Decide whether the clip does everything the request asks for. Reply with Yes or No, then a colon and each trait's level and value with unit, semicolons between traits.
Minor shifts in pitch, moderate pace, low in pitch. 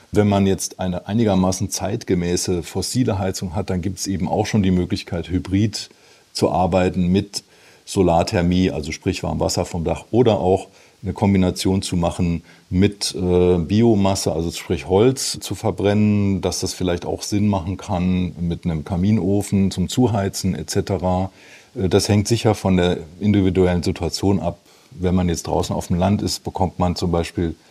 Yes: narrow, 2.1 semitones; average, 160 wpm; very low, 95 Hz